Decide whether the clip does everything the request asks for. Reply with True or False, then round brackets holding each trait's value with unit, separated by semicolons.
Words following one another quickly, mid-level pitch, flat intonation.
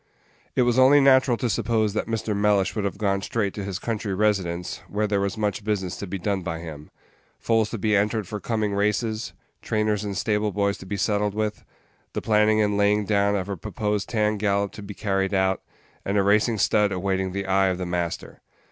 False (210 wpm; 105 Hz; 1.7 semitones)